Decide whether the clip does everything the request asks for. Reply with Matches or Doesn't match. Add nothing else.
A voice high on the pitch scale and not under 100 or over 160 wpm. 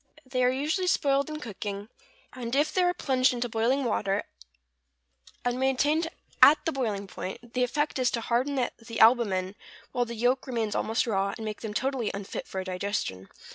Doesn't match